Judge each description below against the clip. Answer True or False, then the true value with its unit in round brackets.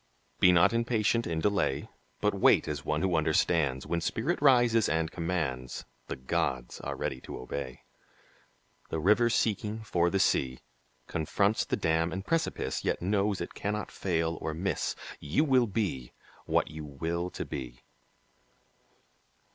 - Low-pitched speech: True (85 Hz)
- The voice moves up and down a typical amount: False (5.8 semitones)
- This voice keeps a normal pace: True (145 wpm)